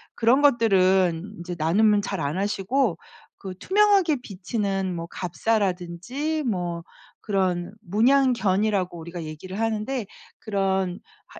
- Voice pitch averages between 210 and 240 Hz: No, high, 195 Hz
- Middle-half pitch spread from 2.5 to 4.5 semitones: Yes, average, 4.1 semitones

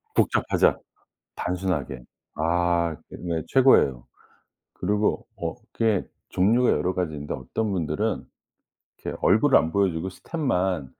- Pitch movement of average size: Yes, average, 4.4 semitones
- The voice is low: Yes, very low, 90 Hz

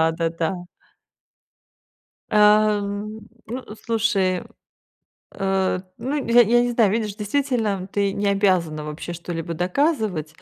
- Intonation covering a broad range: No, average, 4.0 semitones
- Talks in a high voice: Yes, high, 200 Hz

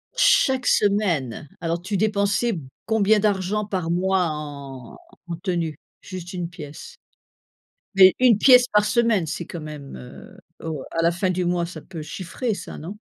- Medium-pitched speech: Yes, medium, 180 Hz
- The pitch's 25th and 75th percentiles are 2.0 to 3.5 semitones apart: No, average, 4.2 semitones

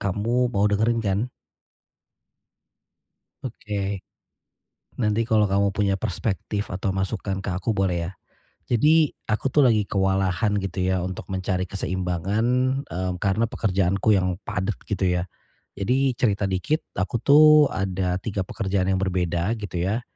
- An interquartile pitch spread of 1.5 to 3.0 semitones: Yes, average, 2.7 semitones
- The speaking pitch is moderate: No, low, 100 Hz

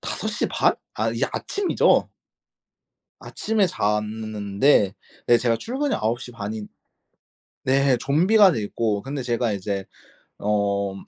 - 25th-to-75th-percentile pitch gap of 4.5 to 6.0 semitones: Yes, average, 5.1 semitones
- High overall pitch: No, low, 115 Hz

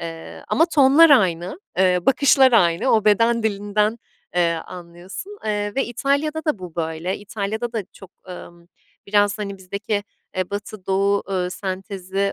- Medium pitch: No, high, 200 Hz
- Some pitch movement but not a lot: Yes, average, 3.9 semitones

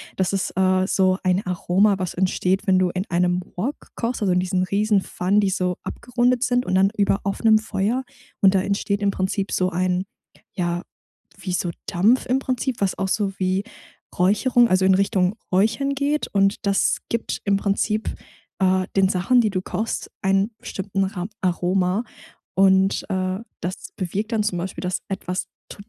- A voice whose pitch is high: Yes, high, 195 Hz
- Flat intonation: Yes, narrow, 2.2 semitones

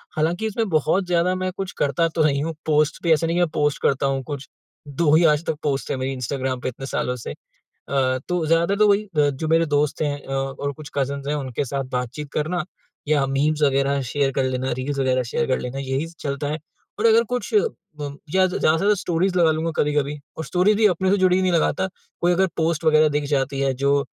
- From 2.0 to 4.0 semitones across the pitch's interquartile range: Yes, average, 3.7 semitones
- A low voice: No, medium, 150 Hz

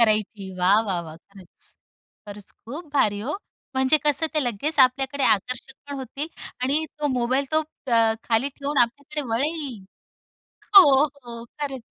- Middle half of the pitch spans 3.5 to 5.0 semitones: Yes, average, 4.6 semitones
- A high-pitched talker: Yes, very high, 260 Hz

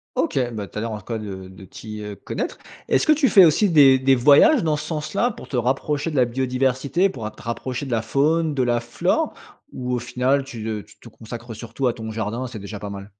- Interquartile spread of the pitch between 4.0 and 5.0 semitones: Yes, average, 4.4 semitones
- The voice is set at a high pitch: No, low, 125 Hz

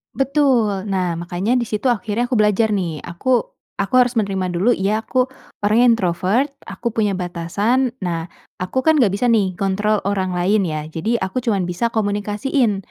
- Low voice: No, high, 205 Hz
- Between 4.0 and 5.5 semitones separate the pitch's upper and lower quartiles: Yes, average, 4.3 semitones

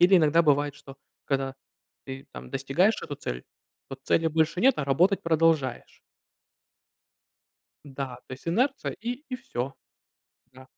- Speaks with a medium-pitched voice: Yes, medium, 150 Hz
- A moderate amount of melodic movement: Yes, average, 4.8 semitones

